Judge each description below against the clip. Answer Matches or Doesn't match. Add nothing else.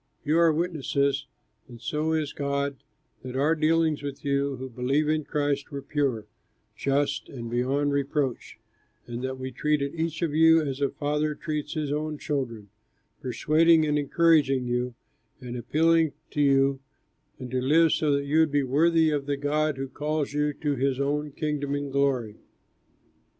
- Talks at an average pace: Matches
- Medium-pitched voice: Matches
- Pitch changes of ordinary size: Doesn't match